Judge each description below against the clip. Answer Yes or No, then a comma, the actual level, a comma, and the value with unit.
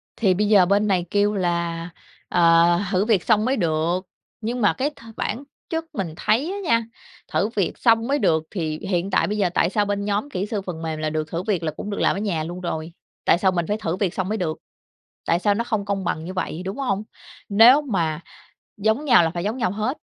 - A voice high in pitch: Yes, high, 195 Hz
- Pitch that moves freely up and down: No, average, 4.0 semitones